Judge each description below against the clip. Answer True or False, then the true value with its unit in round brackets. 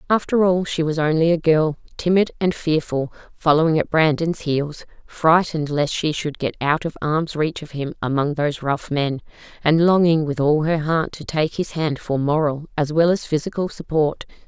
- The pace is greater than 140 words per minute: True (190 wpm)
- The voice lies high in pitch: False (155 Hz)